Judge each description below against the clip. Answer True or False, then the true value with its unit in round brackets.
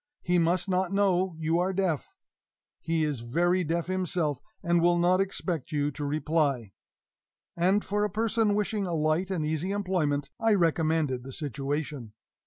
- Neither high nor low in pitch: True (170 Hz)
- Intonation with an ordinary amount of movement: True (3.8 semitones)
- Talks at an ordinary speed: True (160 wpm)